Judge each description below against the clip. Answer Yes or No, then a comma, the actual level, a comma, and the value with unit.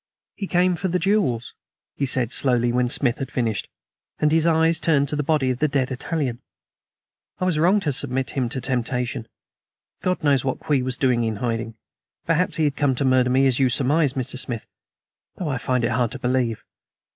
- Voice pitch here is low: Yes, low, 130 Hz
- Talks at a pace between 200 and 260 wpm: Yes, fast, 205 wpm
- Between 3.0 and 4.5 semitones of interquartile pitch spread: Yes, average, 3.7 semitones